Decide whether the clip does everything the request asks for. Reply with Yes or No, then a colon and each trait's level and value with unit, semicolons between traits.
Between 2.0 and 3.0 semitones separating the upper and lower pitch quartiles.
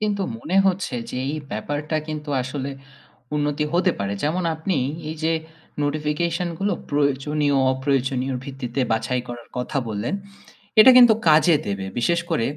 No: average, 4.1 semitones